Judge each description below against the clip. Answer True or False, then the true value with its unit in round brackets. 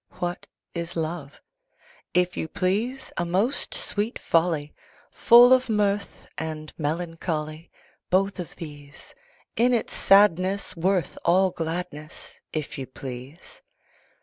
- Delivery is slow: True (115 wpm)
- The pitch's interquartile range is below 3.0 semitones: False (4.1 semitones)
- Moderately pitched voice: True (175 Hz)